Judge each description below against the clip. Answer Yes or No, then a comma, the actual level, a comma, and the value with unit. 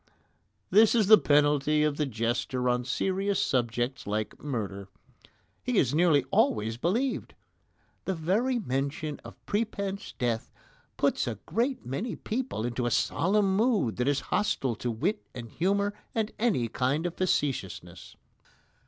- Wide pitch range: Yes, wide, 8.7 semitones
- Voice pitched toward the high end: No, medium, 150 Hz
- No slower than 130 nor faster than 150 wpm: Yes, average, 140 wpm